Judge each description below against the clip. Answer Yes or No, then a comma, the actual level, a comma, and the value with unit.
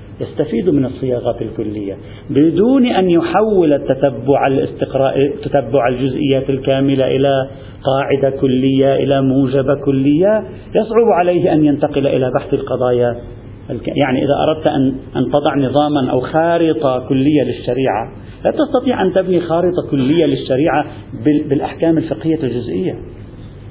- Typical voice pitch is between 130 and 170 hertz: Yes, medium, 140 Hz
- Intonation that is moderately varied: Yes, average, 3.0 semitones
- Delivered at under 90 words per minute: No, average, 115 wpm